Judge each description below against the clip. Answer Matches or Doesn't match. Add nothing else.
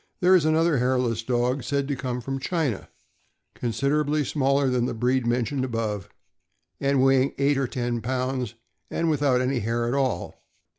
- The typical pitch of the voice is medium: Doesn't match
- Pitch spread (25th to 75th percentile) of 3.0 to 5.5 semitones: Doesn't match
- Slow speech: Doesn't match